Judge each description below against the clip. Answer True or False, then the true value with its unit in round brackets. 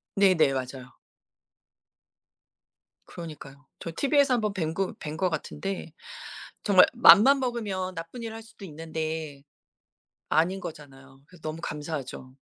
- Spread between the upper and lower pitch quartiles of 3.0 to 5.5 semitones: True (5.1 semitones)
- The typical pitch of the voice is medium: True (165 Hz)